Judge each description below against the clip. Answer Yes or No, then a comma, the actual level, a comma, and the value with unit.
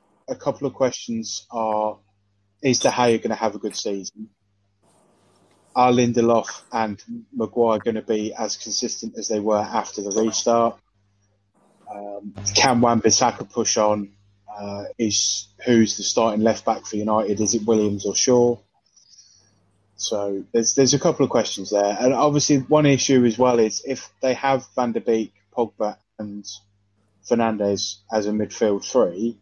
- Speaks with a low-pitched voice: Yes, low, 110 Hz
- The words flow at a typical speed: Yes, average, 155 wpm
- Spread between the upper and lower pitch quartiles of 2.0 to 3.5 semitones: Yes, average, 2.7 semitones